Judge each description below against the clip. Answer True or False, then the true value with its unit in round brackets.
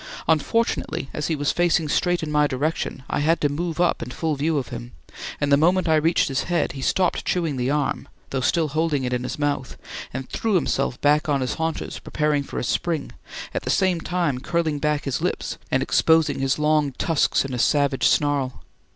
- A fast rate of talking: True (210 wpm)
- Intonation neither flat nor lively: True (3.0 semitones)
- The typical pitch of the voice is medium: True (150 Hz)